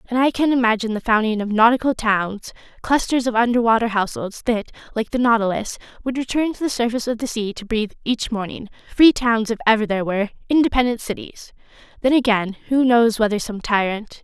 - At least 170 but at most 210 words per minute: Yes, average, 185 wpm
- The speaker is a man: No, female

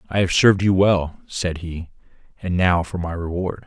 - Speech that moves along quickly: No, average, 195 wpm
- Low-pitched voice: Yes, very low, 90 Hz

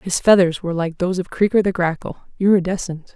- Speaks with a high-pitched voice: No, medium, 180 Hz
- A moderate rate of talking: Yes, average, 170 wpm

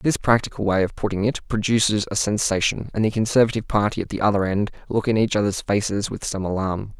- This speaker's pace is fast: Yes, fast, 215 wpm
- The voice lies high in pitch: No, low, 105 Hz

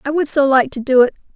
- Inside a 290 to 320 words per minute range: Yes, fast, 310 wpm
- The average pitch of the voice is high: Yes, very high, 270 Hz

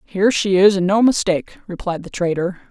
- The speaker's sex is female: Yes, female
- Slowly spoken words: No, average, 200 wpm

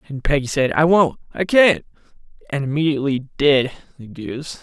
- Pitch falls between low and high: Yes, medium, 145 Hz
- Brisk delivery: No, average, 145 wpm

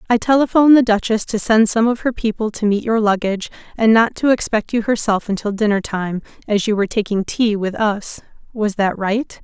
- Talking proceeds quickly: Yes, fast, 210 wpm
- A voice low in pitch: No, high, 215 Hz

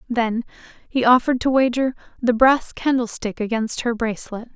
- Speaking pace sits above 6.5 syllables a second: No, 5.2 syllables/s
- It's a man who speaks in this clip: No, female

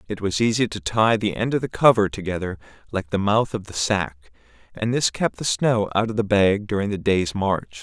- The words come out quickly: Yes, fast, 230 wpm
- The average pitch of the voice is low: Yes, low, 100 Hz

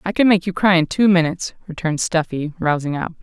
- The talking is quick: Yes, fast, 225 wpm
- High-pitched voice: No, medium, 170 Hz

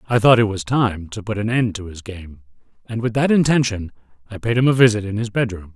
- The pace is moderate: No, fast, 250 wpm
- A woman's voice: No, male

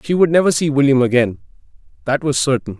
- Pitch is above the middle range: No, medium, 140 Hz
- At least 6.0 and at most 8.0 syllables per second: Yes, 6.4 syllables/s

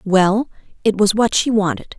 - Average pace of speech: Yes, average, 180 wpm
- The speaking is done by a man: No, female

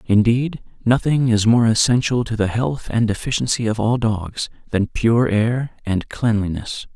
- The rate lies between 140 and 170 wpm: Yes, average, 155 wpm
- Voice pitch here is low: Yes, low, 115 Hz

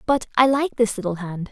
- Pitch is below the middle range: No, high, 225 Hz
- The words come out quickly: Yes, fast, 235 wpm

